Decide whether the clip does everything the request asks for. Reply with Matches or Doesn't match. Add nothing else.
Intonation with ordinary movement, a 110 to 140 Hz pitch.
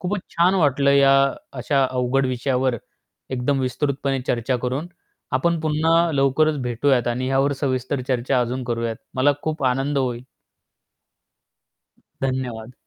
Doesn't match